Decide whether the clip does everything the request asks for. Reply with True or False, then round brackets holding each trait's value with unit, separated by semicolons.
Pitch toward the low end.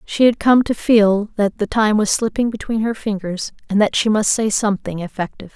False (210 Hz)